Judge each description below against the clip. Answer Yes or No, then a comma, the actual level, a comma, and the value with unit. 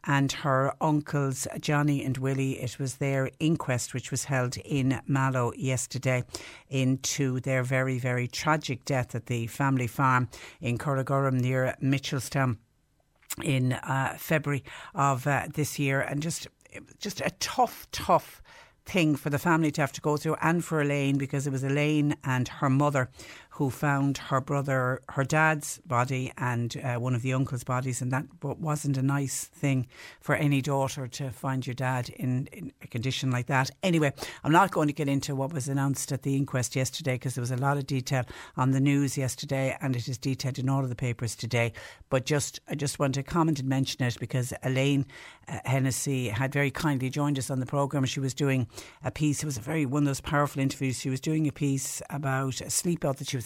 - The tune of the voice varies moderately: No, narrow, 1.9 semitones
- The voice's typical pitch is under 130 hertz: No, low, 135 Hz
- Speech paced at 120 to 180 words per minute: No, average, 200 wpm